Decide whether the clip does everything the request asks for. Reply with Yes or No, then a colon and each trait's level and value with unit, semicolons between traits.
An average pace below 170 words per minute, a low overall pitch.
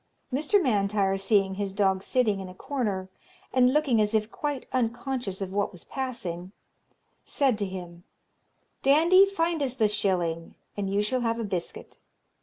No: average, 160 wpm; high, 210 Hz